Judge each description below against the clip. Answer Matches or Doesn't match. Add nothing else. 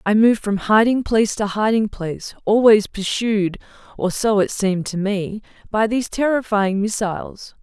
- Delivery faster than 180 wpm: Doesn't match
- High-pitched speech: Matches